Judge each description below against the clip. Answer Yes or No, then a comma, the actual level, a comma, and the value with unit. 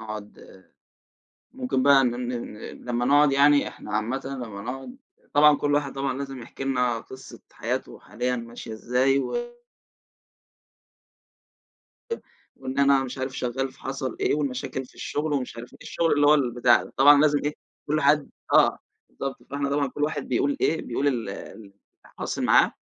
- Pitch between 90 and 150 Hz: Yes, low, 135 Hz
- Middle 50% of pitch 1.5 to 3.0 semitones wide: Yes, average, 2.7 semitones